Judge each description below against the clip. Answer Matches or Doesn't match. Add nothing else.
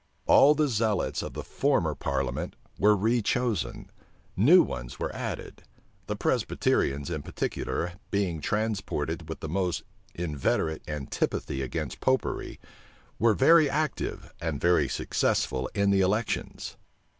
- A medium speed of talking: Doesn't match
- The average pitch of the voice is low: Matches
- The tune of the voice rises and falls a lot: Matches